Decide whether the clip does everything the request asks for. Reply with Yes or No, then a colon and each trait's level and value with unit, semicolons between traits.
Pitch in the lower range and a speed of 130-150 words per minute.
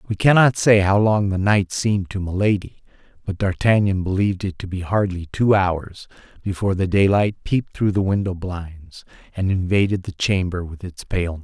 No: very low, 95 Hz; average, 180 wpm